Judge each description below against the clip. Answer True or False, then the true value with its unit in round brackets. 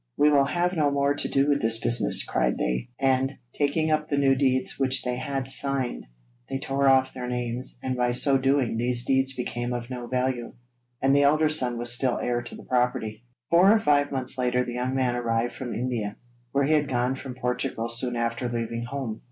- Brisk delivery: True (210 wpm)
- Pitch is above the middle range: False (130 Hz)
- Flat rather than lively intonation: True (2.3 semitones)